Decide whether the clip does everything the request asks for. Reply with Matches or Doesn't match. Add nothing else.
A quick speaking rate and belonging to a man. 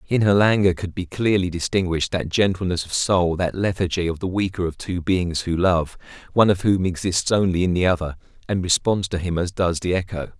Matches